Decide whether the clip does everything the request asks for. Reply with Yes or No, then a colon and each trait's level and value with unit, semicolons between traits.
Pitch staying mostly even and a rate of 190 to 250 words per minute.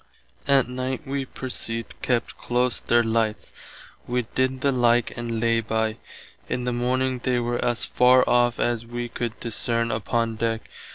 No: narrow, 1.5 semitones; average, 160 wpm